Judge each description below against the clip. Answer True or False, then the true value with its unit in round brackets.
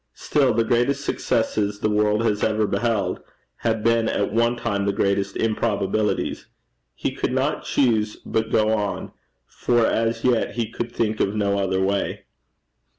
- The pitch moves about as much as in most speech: False (2.2 semitones)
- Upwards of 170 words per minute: False (155 wpm)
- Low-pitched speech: True (110 Hz)